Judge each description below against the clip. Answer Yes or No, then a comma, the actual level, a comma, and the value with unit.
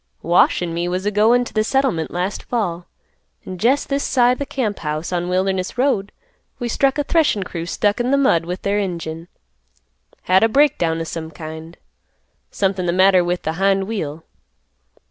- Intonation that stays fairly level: No, wide, 5.5 semitones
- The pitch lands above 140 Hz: Yes, high, 190 Hz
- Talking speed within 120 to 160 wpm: No, average, 185 wpm